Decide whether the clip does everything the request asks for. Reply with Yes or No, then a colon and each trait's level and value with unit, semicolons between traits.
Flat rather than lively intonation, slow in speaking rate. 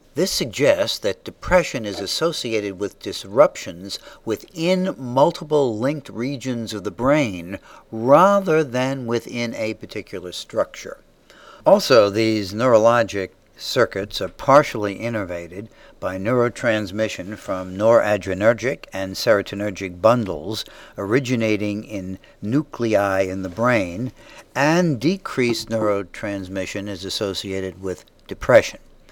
No: average, 4.3 semitones; slow, 100 wpm